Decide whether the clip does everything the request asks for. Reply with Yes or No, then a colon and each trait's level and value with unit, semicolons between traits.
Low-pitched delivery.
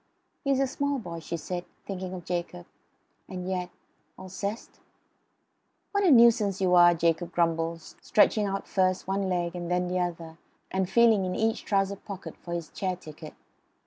No: medium, 185 Hz